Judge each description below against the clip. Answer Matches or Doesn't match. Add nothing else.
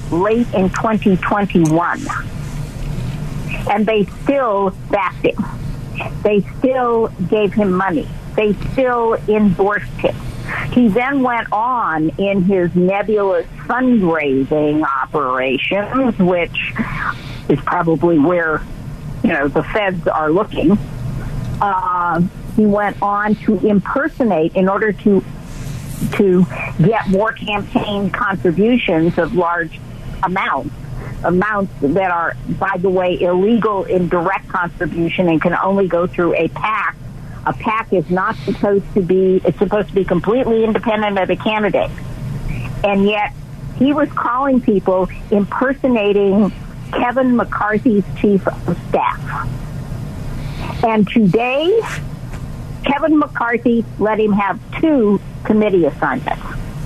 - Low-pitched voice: Doesn't match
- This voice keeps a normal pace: Doesn't match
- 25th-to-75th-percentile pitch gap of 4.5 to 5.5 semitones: Matches